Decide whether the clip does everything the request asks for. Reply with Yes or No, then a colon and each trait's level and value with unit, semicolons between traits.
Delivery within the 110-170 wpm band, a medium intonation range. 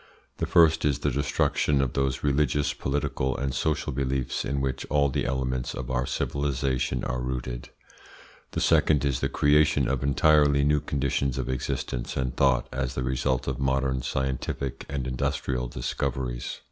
No: average, 160 wpm; narrow, 1.8 semitones